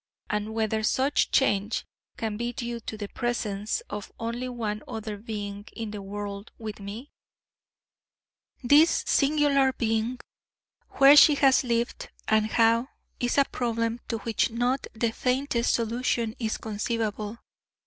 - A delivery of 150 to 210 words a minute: No, slow, 135 wpm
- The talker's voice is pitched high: Yes, high, 230 Hz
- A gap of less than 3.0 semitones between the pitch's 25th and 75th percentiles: Yes, narrow, 2.5 semitones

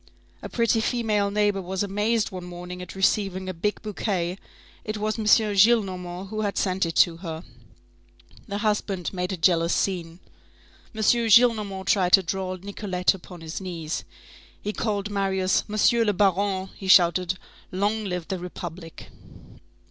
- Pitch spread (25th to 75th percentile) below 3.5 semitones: Yes, narrow, 2.5 semitones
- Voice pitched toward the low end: No, high, 190 Hz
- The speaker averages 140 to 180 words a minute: Yes, average, 150 wpm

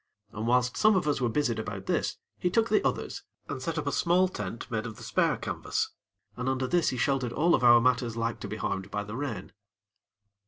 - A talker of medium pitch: No, low, 125 Hz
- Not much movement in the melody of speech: No, average, 4.4 semitones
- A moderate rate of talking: No, fast, 230 wpm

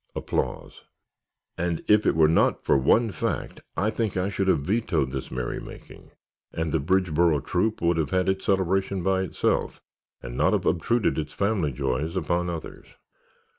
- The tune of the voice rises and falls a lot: No, average, 3.6 semitones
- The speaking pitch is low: Yes, very low, 90 Hz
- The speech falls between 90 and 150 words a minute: No, average, 165 wpm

